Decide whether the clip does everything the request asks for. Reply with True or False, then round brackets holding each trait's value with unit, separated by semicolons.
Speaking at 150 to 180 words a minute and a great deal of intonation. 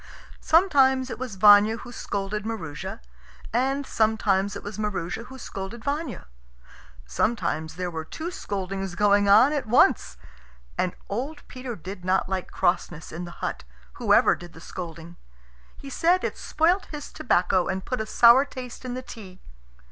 True (155 wpm; 5.7 semitones)